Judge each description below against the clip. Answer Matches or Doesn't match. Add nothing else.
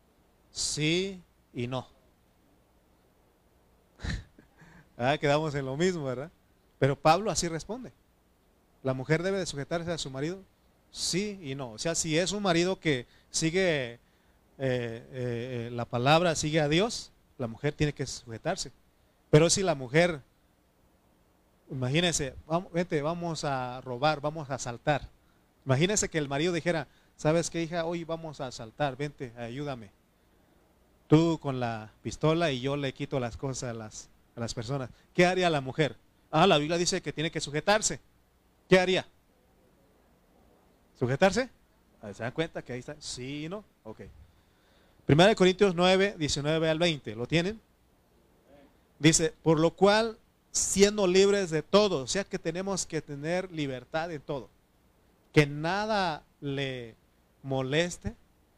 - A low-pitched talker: Doesn't match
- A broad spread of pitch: Matches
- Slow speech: Doesn't match